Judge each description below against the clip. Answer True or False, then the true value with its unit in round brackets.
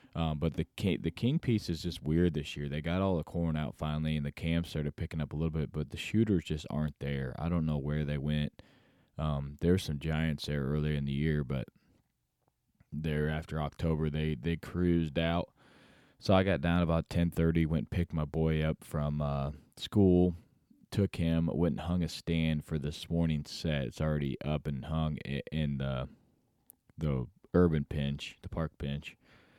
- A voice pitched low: True (80 Hz)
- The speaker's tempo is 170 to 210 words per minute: True (195 wpm)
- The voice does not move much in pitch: True (2.2 semitones)